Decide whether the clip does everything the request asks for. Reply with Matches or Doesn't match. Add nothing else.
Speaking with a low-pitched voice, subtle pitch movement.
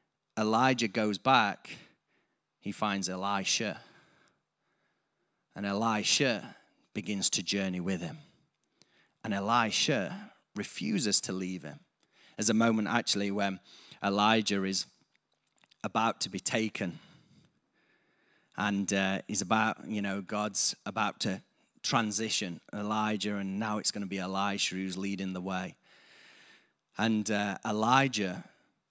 Matches